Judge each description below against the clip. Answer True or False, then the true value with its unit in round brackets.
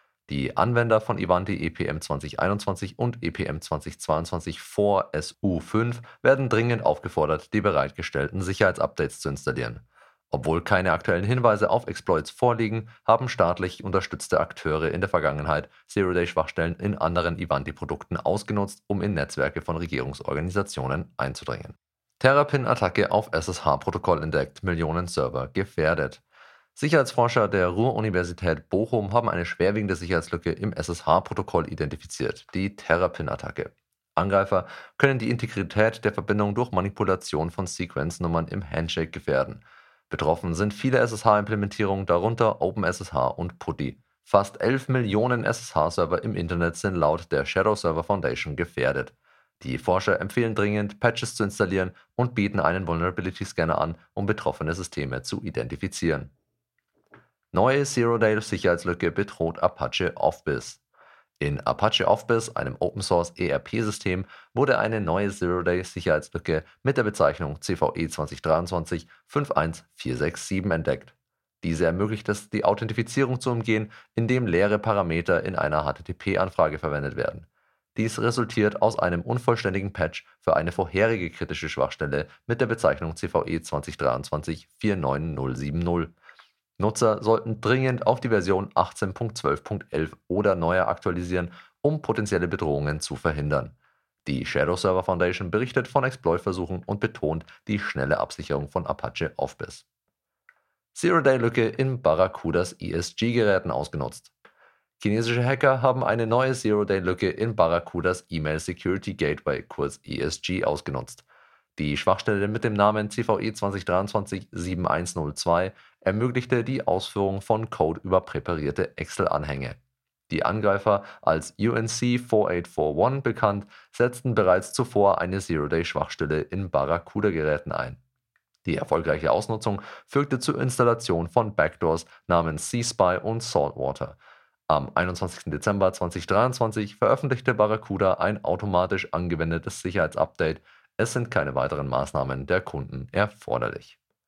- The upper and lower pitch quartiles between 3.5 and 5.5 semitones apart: True (5.0 semitones)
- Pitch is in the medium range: False (95 Hz)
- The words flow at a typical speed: False (115 wpm)